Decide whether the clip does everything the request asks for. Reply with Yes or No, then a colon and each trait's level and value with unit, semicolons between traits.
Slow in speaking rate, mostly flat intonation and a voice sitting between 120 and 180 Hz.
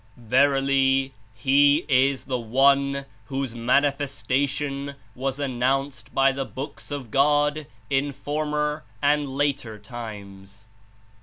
Yes: slow, 105 wpm; narrow, 2.0 semitones; low, 135 Hz